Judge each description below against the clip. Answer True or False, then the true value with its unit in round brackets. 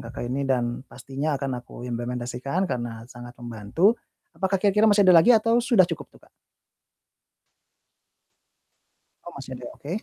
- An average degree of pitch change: False (7.4 semitones)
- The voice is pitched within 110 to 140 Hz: True (135 Hz)